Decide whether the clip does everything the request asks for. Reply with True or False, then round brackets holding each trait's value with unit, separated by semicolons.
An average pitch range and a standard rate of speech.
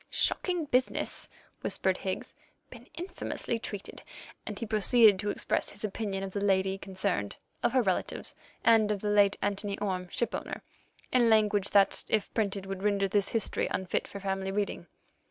False (2.3 semitones; 160 wpm)